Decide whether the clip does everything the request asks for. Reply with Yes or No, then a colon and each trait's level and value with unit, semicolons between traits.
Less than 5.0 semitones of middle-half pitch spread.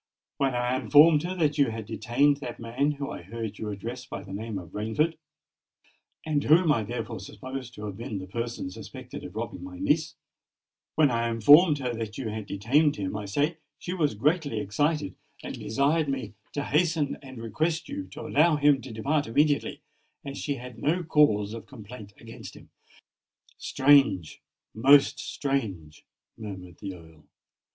No: wide, 5.6 semitones